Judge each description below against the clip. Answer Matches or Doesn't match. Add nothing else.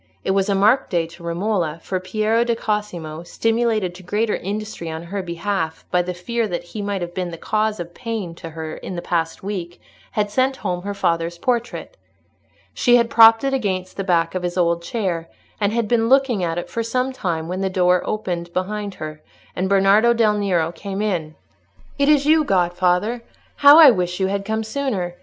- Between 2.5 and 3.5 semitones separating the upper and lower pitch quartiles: Doesn't match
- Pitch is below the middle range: Doesn't match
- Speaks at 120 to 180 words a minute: Doesn't match